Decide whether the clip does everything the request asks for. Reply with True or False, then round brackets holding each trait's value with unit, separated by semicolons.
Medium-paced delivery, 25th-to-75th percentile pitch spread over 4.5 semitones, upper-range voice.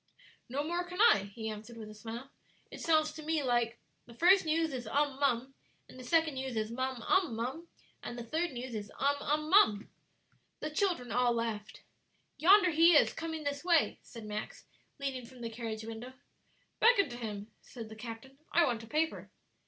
True (190 wpm; 5.5 semitones; 260 Hz)